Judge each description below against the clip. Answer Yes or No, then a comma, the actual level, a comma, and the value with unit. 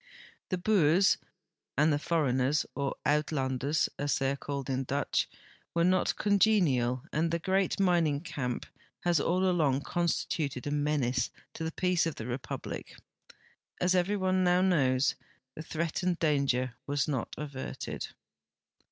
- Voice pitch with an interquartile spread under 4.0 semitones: No, average, 4.5 semitones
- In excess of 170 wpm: No, average, 145 wpm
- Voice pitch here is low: No, medium, 150 Hz